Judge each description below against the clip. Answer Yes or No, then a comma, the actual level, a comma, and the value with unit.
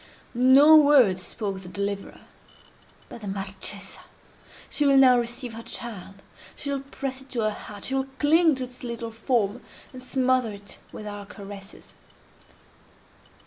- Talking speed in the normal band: Yes, average, 145 wpm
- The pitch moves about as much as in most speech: Yes, average, 4.7 semitones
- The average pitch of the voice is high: Yes, high, 235 Hz